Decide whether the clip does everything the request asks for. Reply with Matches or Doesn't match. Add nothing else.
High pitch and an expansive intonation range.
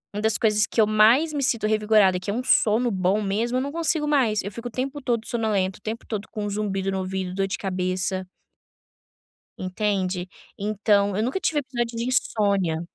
Doesn't match